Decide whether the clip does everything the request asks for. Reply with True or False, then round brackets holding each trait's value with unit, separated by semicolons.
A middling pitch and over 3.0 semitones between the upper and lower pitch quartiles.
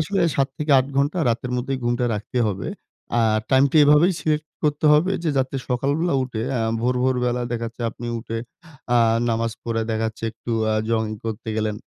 False (125 Hz; 4.1 semitones)